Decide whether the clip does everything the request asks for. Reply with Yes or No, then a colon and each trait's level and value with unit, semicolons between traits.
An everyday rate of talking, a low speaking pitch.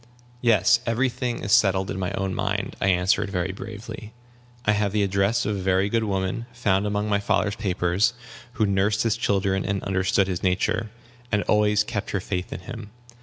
Yes: average, 190 wpm; low, 100 Hz